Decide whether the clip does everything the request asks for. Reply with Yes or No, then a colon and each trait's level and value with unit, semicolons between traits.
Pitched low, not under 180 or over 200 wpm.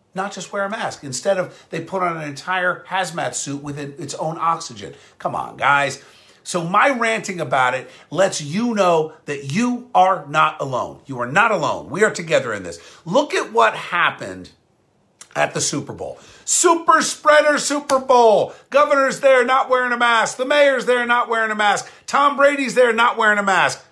No: high, 200 Hz; average, 190 wpm